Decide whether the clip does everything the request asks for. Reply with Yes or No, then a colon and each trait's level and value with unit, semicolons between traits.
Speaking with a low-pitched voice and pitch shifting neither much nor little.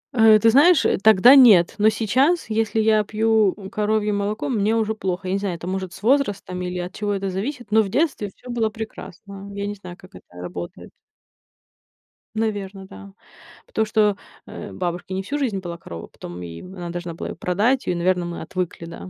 No: high, 200 Hz; average, 3.4 semitones